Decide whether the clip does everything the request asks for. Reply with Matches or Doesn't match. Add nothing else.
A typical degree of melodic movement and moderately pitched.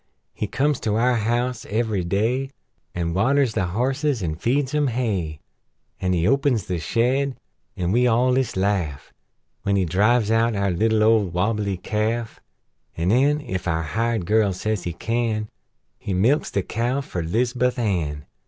Doesn't match